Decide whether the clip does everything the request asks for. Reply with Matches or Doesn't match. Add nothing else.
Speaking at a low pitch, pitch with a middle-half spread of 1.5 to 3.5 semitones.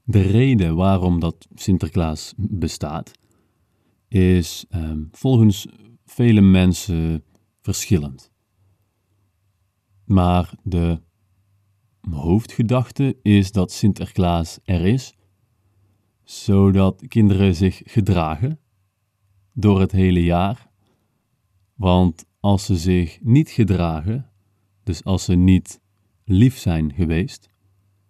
Matches